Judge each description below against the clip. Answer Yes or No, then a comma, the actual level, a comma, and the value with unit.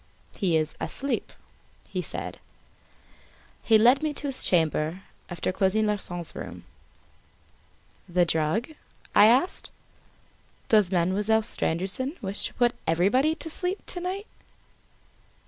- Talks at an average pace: No, slow, 115 wpm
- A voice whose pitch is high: Yes, high, 210 Hz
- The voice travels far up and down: Yes, wide, 6.9 semitones